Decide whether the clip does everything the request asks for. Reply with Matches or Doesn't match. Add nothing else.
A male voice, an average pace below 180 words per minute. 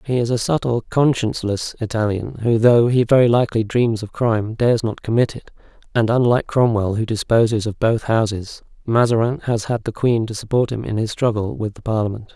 Doesn't match